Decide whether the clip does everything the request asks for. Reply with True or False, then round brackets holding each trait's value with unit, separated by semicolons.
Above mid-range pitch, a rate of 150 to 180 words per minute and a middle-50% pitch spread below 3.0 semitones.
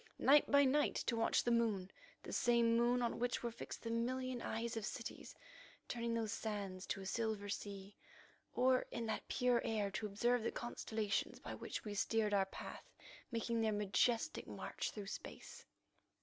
True (230 Hz; 175 wpm; 2.5 semitones)